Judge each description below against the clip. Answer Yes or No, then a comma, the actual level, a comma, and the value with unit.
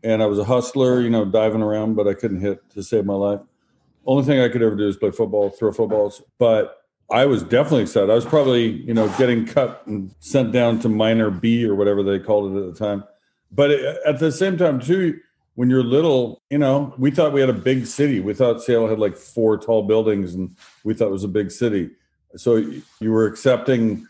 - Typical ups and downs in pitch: Yes, average, 3.8 semitones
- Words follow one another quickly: Yes, fast, 230 wpm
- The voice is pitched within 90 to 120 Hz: Yes, low, 115 Hz